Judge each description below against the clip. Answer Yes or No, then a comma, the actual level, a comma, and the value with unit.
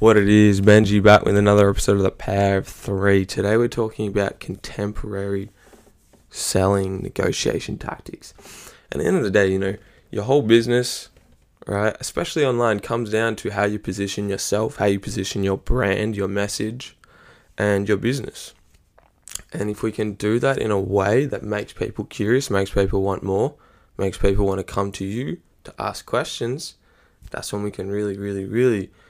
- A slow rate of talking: No, average, 175 wpm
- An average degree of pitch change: No, narrow, 1.9 semitones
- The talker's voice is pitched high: No, low, 100 Hz